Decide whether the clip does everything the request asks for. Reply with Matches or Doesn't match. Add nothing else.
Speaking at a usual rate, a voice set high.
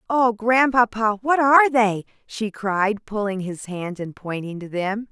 Matches